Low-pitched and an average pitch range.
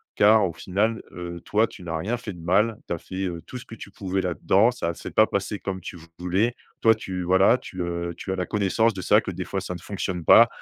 Yes: very low, 95 Hz; average, 3.3 semitones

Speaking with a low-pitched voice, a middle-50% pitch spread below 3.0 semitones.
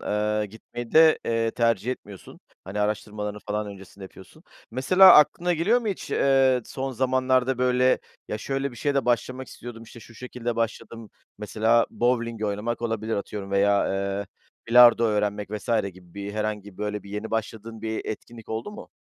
No: low, 115 Hz; average, 3.3 semitones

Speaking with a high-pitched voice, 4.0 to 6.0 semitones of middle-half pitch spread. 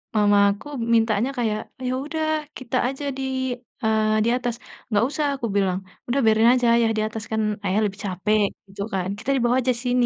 No: high, 220 Hz; average, 2.9 semitones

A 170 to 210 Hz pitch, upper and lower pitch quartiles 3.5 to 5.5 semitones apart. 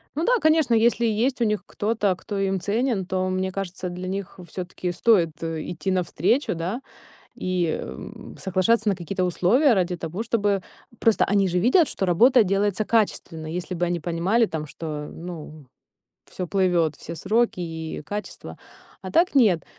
Yes: high, 190 Hz; average, 4.2 semitones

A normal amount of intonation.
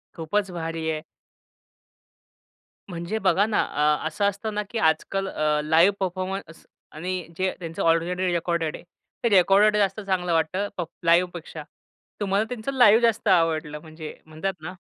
Yes: average, 3.4 semitones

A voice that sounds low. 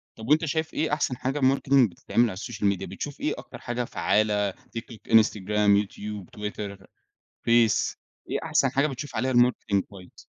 Yes: low, 115 Hz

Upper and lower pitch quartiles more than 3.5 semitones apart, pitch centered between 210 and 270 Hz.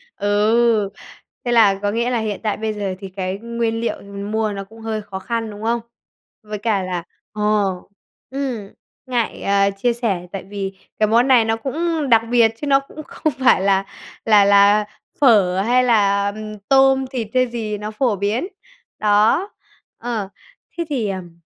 No: average, 3.1 semitones; high, 215 Hz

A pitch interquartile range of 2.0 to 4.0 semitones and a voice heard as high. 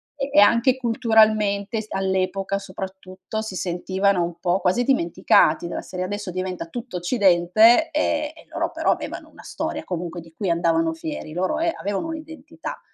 No: average, 4.6 semitones; high, 195 Hz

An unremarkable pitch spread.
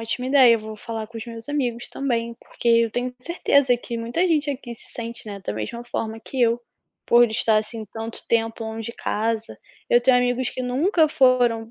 No: narrow, 2.0 semitones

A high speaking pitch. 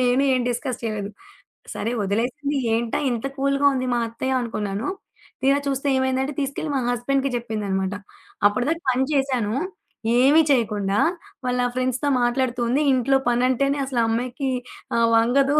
Yes: very high, 255 Hz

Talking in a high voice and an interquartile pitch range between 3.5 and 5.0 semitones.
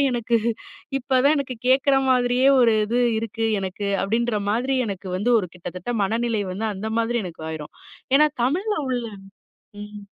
Yes: high, 235 Hz; average, 3.8 semitones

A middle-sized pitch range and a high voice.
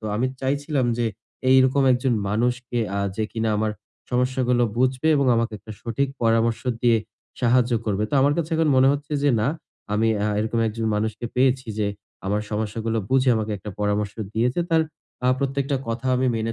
No: average, 3.0 semitones; low, 120 Hz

